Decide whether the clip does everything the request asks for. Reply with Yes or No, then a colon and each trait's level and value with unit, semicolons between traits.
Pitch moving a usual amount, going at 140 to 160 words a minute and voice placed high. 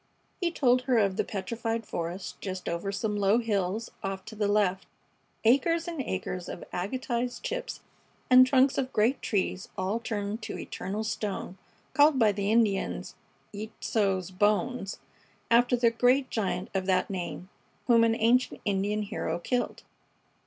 Yes: average, 4.0 semitones; average, 150 wpm; high, 215 Hz